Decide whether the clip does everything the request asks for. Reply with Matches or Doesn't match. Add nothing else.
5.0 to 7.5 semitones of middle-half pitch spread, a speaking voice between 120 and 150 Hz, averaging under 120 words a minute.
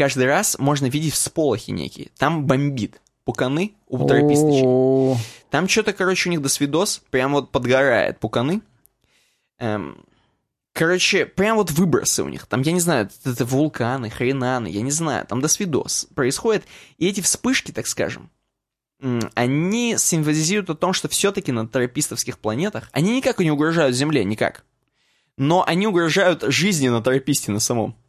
Doesn't match